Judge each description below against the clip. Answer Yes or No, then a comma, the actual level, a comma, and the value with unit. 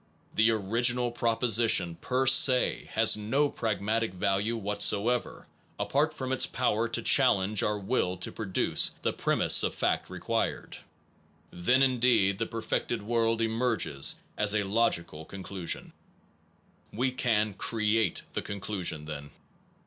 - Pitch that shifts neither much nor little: Yes, average, 3.6 semitones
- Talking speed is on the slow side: Yes, slow, 130 wpm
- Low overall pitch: Yes, low, 110 Hz